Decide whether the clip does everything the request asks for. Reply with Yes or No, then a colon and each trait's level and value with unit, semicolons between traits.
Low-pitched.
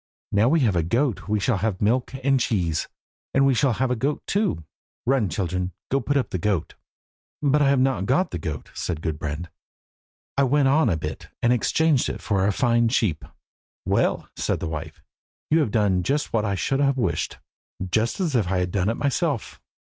Yes: low, 115 Hz